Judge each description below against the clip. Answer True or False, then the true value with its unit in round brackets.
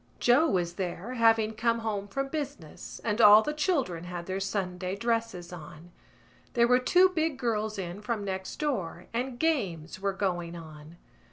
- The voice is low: False (210 Hz)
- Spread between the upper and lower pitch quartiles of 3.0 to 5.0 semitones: False (5.4 semitones)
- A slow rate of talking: False (165 wpm)